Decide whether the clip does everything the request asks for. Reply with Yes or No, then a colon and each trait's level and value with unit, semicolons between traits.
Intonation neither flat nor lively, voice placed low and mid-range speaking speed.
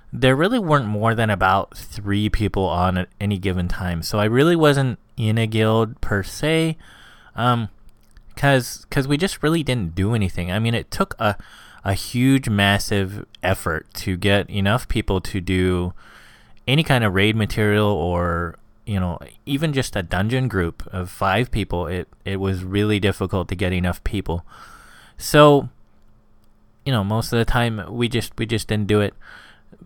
Yes: average, 3.5 semitones; low, 105 Hz; average, 170 wpm